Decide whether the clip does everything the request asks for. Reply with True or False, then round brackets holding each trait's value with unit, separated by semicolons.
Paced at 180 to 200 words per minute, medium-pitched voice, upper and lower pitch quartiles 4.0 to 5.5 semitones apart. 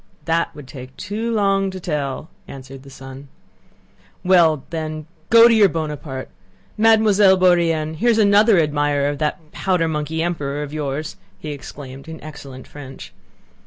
False (150 wpm; 155 Hz; 4.8 semitones)